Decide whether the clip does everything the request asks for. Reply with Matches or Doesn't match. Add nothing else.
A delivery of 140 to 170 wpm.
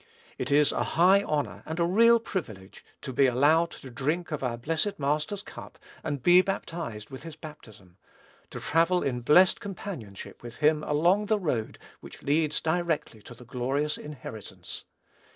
Matches